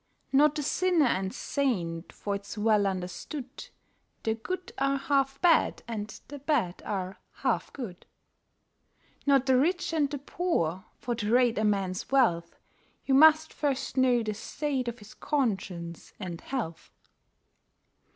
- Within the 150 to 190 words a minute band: No, average, 140 wpm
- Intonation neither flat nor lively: No, wide, 6.0 semitones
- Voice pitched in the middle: No, high, 245 Hz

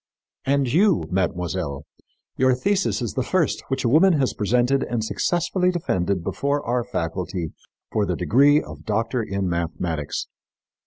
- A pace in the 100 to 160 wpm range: Yes, average, 145 wpm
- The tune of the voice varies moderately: No, wide, 7.4 semitones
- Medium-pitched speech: No, low, 120 Hz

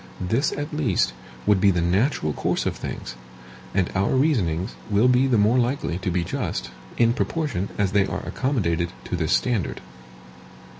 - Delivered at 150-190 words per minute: Yes, average, 165 wpm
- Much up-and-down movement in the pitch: Yes, wide, 6.1 semitones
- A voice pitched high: No, low, 105 Hz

